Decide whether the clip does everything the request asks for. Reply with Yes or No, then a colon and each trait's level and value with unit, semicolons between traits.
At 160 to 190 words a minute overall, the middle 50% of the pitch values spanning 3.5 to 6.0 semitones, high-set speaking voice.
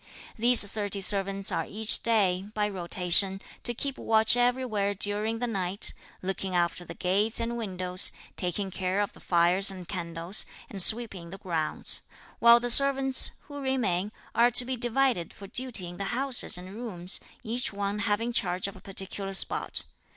Yes: average, 165 wpm; average, 4.1 semitones; high, 200 Hz